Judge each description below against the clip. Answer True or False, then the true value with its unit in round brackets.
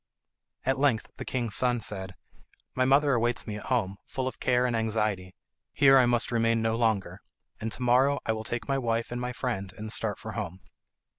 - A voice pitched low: True (115 Hz)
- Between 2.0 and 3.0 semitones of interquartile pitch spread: True (2.7 semitones)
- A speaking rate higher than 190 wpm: True (205 wpm)